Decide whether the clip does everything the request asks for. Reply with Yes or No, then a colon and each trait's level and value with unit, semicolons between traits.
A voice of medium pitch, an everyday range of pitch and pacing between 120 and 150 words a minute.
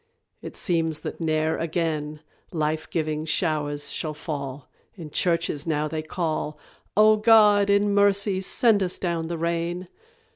Yes: medium, 165 Hz; average, 3.5 semitones; average, 140 wpm